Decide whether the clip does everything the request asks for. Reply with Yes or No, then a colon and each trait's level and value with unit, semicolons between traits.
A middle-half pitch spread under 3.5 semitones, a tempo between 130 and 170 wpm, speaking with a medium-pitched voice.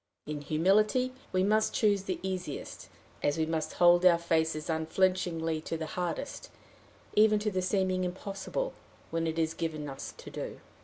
Yes: average, 3.1 semitones; average, 160 wpm; medium, 175 Hz